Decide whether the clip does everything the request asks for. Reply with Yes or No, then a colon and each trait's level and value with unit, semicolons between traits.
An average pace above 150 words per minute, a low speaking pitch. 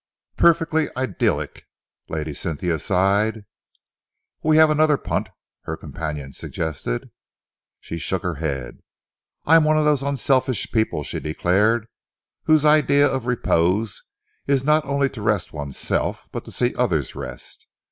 No: slow, 135 wpm; low, 110 Hz